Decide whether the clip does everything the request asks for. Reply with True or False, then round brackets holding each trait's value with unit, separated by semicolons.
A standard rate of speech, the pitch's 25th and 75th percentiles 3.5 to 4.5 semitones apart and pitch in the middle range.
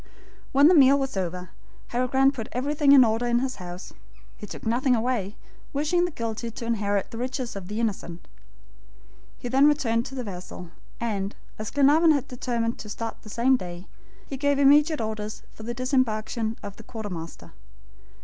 False (180 wpm; 4.0 semitones; 235 Hz)